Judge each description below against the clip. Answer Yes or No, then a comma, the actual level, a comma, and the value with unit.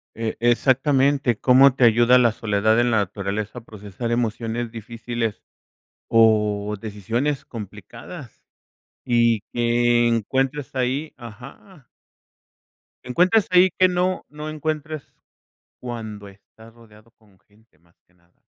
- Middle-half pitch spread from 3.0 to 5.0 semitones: Yes, average, 3.5 semitones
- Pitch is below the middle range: Yes, low, 120 Hz